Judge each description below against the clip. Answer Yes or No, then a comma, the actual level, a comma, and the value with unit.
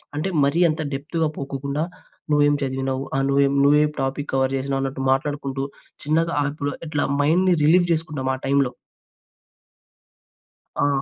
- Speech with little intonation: Yes, narrow, 2.0 semitones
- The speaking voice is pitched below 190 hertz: Yes, medium, 140 Hz